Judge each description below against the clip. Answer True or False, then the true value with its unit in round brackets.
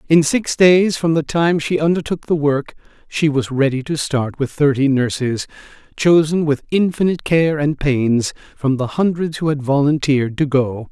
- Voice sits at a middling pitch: True (150 Hz)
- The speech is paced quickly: False (175 wpm)